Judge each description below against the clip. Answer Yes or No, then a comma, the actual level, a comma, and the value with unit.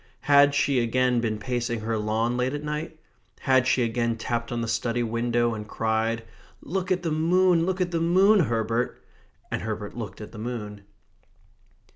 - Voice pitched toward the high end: No, low, 120 Hz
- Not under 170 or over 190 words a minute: Yes, average, 175 wpm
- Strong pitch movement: No, average, 4.9 semitones